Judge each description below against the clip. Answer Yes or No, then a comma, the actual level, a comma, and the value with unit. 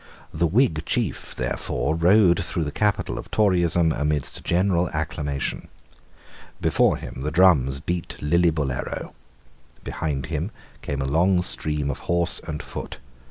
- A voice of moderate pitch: No, very low, 80 Hz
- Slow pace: Yes, slow, 130 wpm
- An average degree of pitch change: Yes, average, 3.1 semitones